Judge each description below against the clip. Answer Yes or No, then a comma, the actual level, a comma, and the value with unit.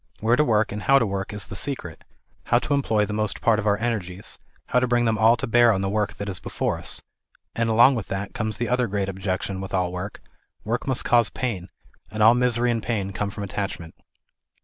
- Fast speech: Yes, fast, 240 wpm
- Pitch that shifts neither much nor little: Yes, average, 3.4 semitones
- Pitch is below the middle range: Yes, low, 110 Hz